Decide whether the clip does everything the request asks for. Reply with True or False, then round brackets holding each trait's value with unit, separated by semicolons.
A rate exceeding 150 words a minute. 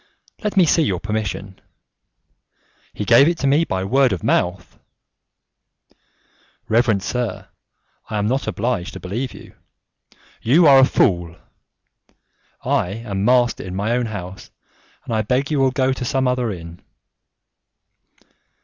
False (140 wpm)